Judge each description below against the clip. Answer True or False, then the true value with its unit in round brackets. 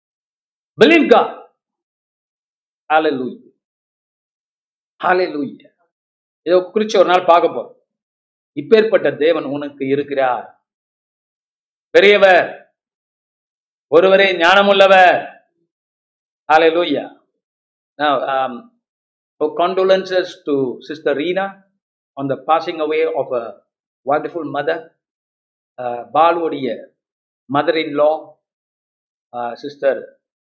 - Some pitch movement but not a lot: False (6.3 semitones)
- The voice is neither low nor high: True (155 Hz)